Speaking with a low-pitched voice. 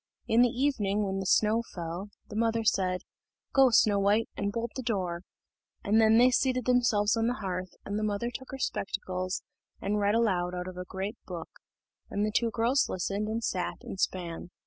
No: high, 210 Hz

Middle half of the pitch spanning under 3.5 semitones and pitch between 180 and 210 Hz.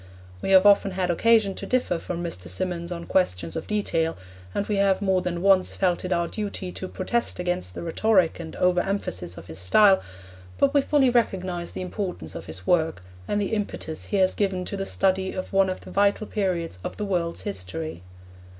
Yes: average, 3.0 semitones; medium, 185 Hz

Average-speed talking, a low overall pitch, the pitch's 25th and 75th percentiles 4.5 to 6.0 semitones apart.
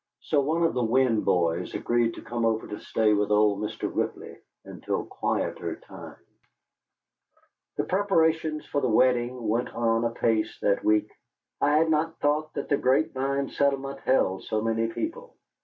Yes: average, 160 wpm; low, 125 Hz; average, 4.9 semitones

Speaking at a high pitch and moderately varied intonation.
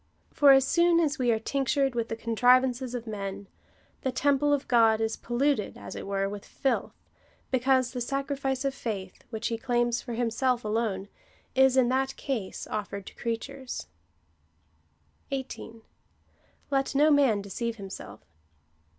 Yes: high, 245 Hz; average, 3.4 semitones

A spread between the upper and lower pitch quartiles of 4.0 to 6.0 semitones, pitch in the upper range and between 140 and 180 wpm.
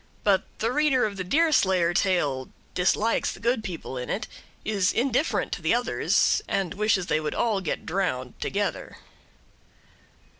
Yes: average, 4.5 semitones; high, 195 Hz; average, 150 wpm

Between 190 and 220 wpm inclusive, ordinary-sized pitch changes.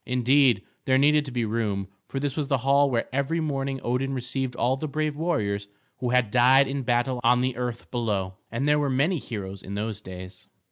Yes: fast, 205 wpm; average, 3.1 semitones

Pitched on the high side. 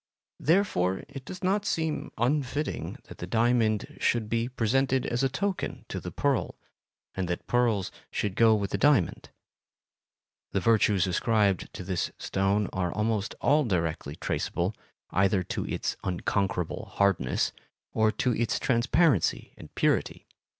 No: low, 110 Hz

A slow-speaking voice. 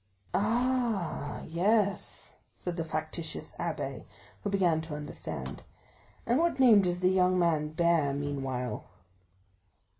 Yes: slow, 115 wpm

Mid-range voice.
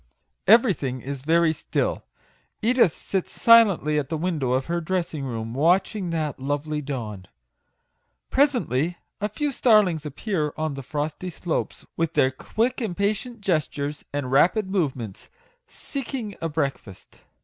Yes: medium, 160 Hz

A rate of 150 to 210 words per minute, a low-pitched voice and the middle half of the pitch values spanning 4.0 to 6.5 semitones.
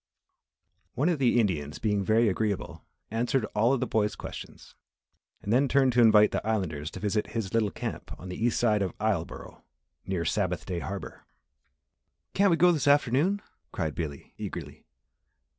Yes: average, 165 wpm; low, 110 Hz; average, 4.7 semitones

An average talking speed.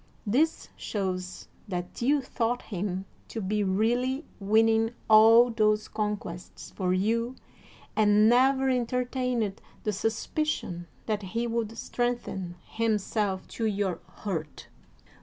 No: slow, 110 wpm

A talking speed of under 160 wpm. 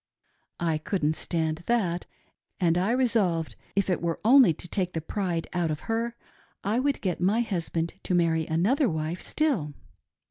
No: average, 165 wpm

